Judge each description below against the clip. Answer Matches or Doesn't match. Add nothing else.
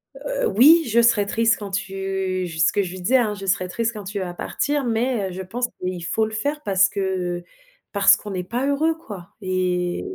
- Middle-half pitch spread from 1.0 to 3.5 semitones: Doesn't match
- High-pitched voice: Matches